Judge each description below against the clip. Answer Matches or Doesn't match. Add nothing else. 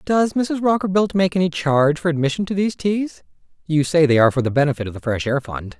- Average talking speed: Doesn't match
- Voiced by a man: Matches